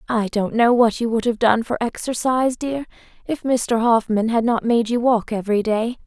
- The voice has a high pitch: Yes, high, 230 Hz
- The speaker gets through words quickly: Yes, fast, 210 wpm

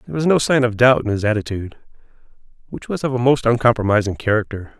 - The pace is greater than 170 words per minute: Yes, average, 200 wpm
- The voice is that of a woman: No, male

